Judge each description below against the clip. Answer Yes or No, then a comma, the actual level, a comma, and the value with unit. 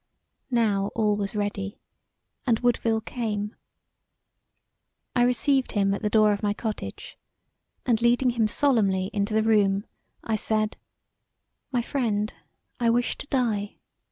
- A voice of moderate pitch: No, high, 220 Hz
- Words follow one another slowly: Yes, slow, 130 wpm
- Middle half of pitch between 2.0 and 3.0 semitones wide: Yes, narrow, 2.6 semitones